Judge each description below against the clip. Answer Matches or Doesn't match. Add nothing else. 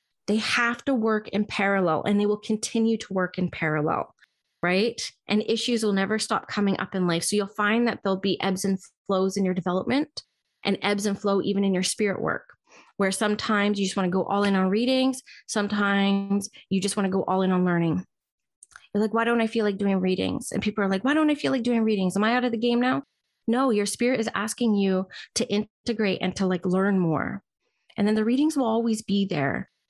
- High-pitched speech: Matches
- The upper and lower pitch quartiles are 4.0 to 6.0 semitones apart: Doesn't match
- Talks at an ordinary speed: Doesn't match